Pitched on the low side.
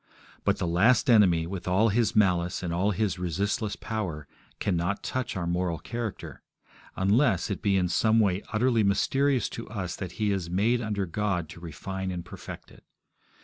Yes: very low, 95 Hz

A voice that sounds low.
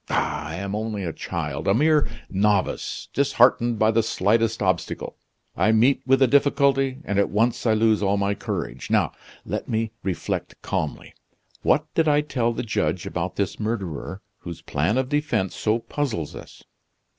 Yes: low, 110 Hz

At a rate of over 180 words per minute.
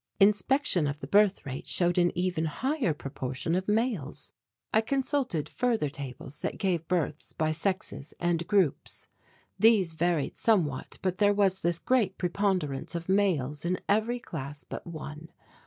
No: average, 150 wpm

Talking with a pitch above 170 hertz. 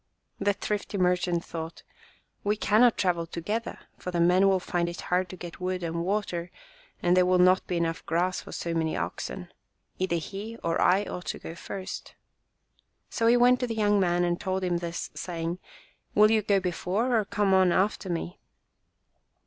Yes: medium, 185 Hz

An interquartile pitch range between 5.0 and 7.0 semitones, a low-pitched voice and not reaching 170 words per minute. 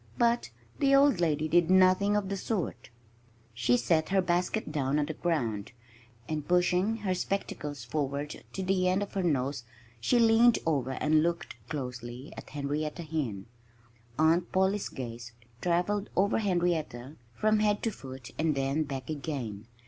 No: wide, 5.6 semitones; medium, 160 Hz; average, 155 wpm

